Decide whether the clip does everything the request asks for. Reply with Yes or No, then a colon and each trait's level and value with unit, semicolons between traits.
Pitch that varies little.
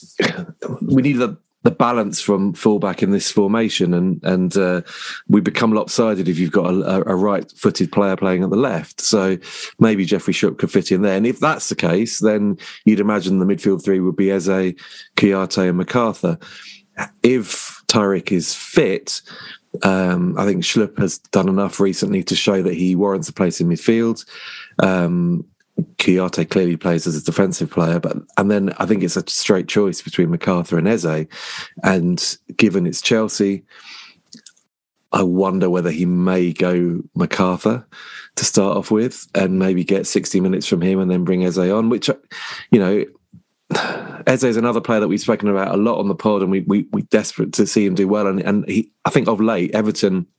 Yes: narrow, 2.3 semitones